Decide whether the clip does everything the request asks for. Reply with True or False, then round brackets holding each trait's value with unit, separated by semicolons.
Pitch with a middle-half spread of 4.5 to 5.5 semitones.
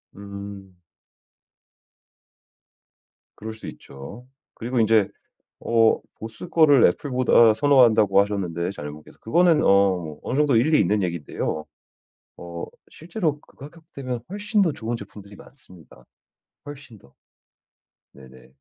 False (6.6 semitones)